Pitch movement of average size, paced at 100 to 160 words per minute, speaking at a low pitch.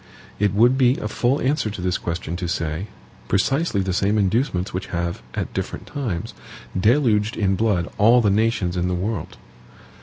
No: average, 4.2 semitones; average, 175 wpm; low, 100 Hz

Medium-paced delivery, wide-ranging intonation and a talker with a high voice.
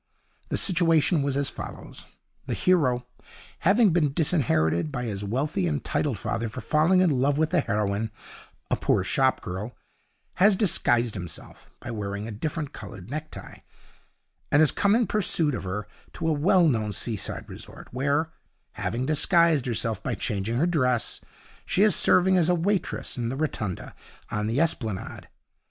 No: average, 160 wpm; wide, 6.8 semitones; medium, 140 Hz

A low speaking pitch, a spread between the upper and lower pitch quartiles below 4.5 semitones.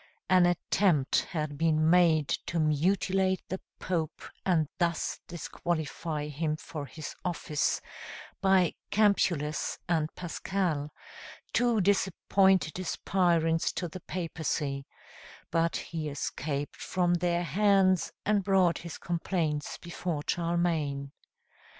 No: medium, 170 Hz; average, 3.2 semitones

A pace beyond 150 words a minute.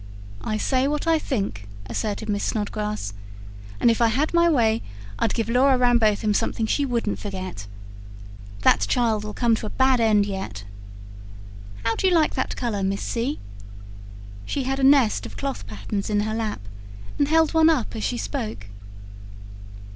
Yes: average, 165 wpm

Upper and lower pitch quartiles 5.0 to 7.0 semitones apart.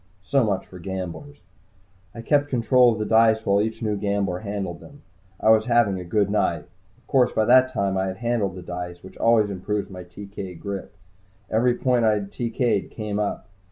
No: average, 3.5 semitones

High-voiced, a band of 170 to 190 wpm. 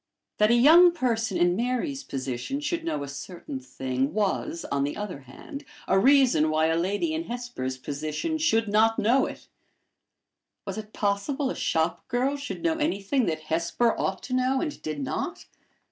Yes: high, 215 Hz; average, 175 wpm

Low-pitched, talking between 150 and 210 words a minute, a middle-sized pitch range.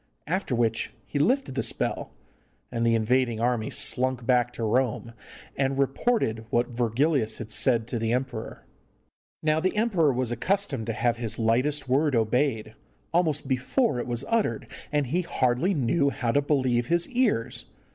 Yes: low, 130 Hz; average, 160 wpm; average, 4.2 semitones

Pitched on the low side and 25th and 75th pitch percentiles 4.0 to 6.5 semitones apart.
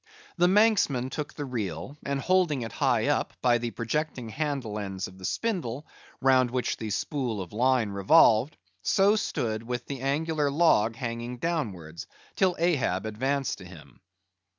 Yes: low, 125 Hz; wide, 5.4 semitones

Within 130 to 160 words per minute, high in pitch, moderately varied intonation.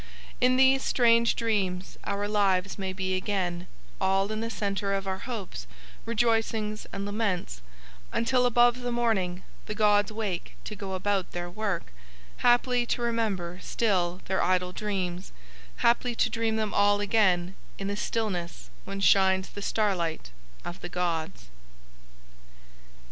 Yes: average, 140 wpm; high, 200 Hz; average, 3.3 semitones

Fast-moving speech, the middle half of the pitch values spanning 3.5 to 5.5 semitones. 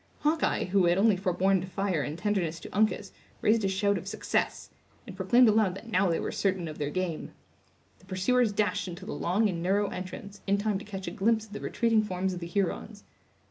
No: fast, 220 wpm; narrow, 2.5 semitones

